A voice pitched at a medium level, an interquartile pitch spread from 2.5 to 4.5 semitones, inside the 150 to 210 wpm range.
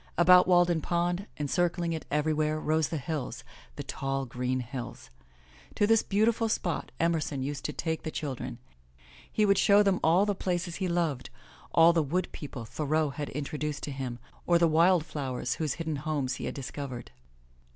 Yes: medium, 155 Hz; average, 3.7 semitones; average, 170 wpm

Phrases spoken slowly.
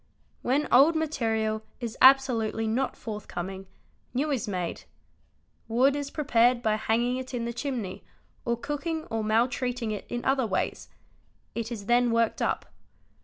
No: average, 145 wpm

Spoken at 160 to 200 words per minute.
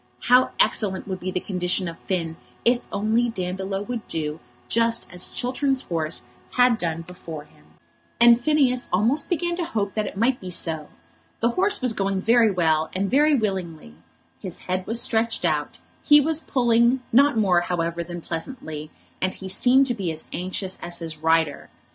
Yes: average, 175 wpm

